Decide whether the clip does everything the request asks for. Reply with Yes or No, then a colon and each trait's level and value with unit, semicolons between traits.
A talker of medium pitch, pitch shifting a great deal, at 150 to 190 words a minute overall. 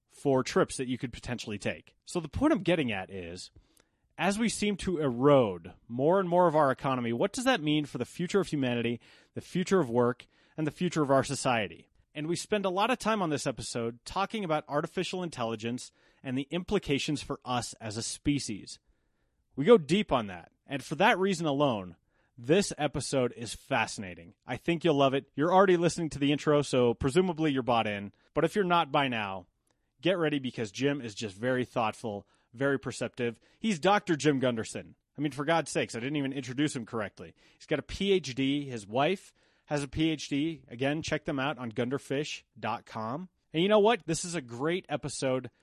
No: medium, 145 Hz; wide, 5.7 semitones; average, 200 wpm